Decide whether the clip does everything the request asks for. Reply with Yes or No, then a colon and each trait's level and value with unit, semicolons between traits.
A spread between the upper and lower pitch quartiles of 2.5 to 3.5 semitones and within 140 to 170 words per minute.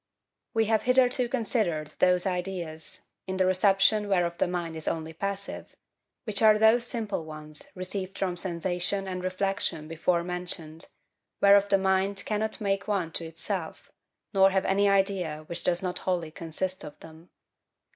Yes: average, 2.8 semitones; average, 155 wpm